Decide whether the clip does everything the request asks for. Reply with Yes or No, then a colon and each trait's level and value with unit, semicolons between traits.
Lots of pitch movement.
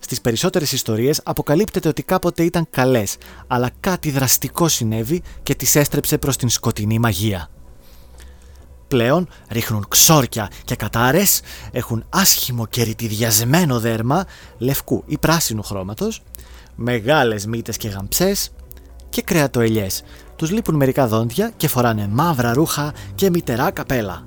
Yes: wide, 6.0 semitones